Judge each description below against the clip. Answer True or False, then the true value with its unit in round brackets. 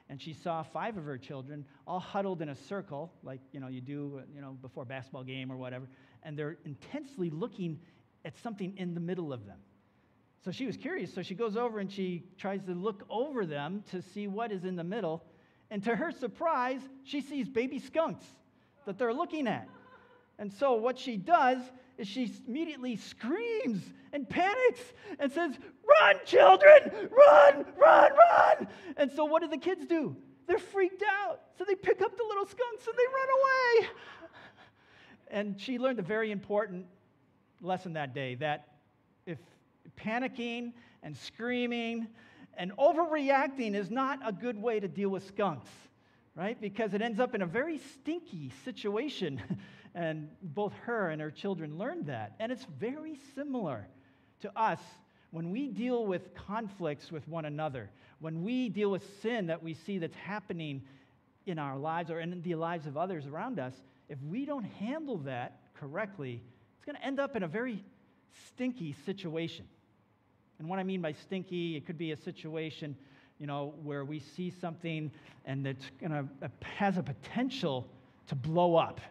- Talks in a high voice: True (195 Hz)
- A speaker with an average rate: True (175 wpm)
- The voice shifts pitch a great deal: True (8.6 semitones)